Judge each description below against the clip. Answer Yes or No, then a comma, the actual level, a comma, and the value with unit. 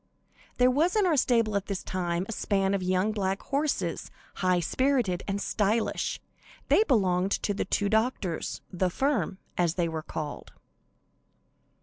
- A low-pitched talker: No, high, 200 Hz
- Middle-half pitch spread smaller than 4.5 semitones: No, average, 5.1 semitones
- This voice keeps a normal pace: Yes, average, 150 wpm